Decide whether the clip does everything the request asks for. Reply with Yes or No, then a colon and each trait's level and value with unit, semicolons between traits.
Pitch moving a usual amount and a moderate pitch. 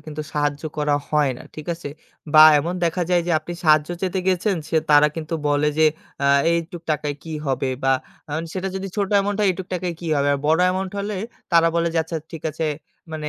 Yes: average, 3.2 semitones; medium, 165 Hz